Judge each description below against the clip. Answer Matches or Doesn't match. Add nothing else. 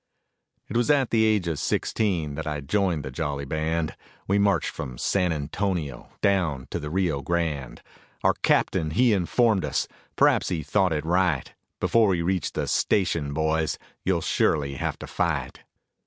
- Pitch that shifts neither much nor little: Matches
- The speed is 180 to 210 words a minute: Doesn't match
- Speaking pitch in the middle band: Doesn't match